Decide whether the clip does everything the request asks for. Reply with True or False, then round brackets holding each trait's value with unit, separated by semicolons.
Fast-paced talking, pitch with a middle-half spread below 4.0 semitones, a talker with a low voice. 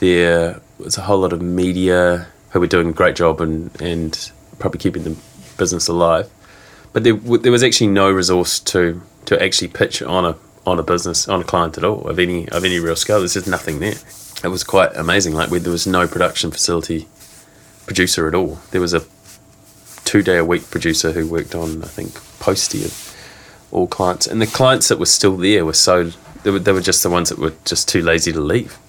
True (220 wpm; 2.4 semitones; 90 Hz)